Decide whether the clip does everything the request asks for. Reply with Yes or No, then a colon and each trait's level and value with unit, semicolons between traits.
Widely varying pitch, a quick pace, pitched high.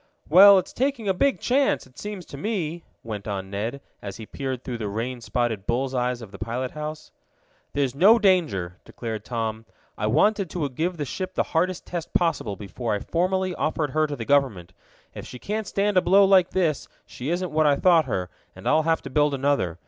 No: wide, 7.8 semitones; fast, 210 wpm; medium, 145 Hz